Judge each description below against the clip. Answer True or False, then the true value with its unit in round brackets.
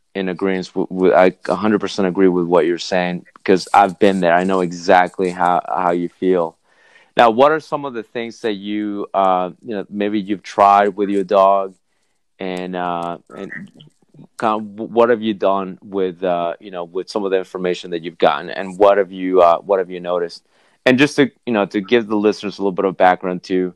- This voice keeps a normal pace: False (215 wpm)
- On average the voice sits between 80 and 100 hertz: True (95 Hz)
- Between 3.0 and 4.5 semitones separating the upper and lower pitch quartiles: False (2.5 semitones)